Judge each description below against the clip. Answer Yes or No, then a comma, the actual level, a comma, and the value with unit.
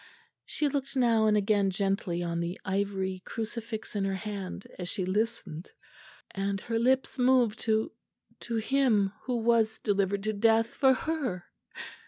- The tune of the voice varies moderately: Yes, average, 3.2 semitones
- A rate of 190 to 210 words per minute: No, average, 150 wpm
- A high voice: Yes, high, 215 Hz